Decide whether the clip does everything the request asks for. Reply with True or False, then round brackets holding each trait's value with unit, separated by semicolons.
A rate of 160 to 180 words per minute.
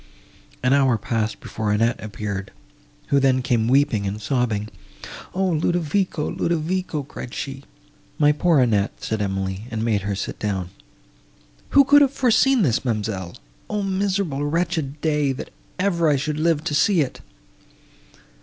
False (140 wpm)